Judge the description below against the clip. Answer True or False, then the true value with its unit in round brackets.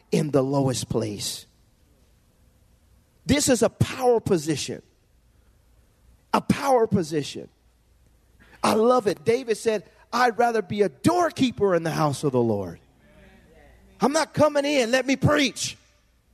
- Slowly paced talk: True (130 wpm)